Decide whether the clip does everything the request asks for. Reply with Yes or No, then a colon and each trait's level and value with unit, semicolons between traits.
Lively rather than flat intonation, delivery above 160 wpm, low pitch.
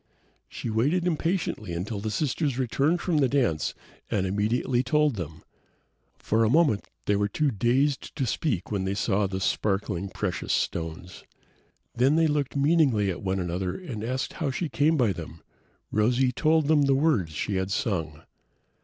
Yes: wide, 7.0 semitones; average, 170 wpm; low, 115 Hz